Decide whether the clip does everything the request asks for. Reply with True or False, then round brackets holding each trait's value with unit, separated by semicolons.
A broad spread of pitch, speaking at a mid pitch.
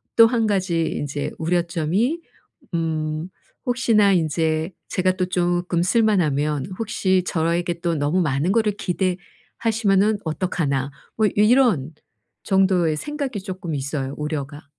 False (4.6 semitones; 175 Hz)